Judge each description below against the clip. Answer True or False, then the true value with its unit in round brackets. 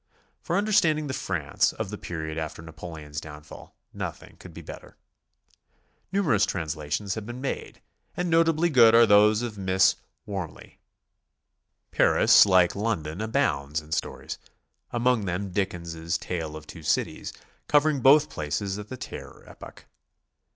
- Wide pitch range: True (7.5 semitones)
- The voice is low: True (100 Hz)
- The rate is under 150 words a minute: True (140 wpm)